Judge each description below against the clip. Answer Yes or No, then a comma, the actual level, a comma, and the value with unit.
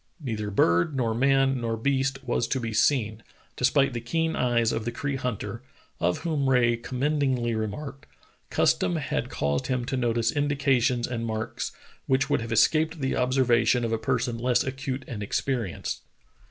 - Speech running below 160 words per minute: No, average, 165 wpm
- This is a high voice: No, low, 125 Hz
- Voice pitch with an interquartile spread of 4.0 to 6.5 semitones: No, average, 2.9 semitones